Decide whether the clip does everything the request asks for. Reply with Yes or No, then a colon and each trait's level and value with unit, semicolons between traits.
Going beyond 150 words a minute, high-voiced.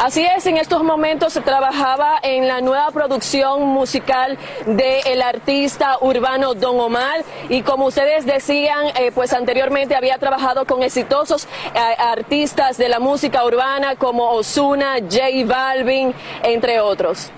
No: average, 140 wpm; very high, 265 Hz